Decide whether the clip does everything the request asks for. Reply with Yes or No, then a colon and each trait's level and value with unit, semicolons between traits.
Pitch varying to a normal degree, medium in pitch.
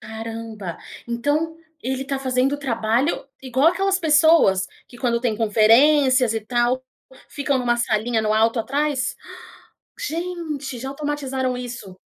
No: average, 4.1 semitones; very high, 255 Hz